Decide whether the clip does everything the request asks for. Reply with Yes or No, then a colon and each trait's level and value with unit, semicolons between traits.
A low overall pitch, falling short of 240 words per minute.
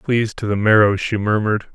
Yes: low, 105 Hz; fast, 205 wpm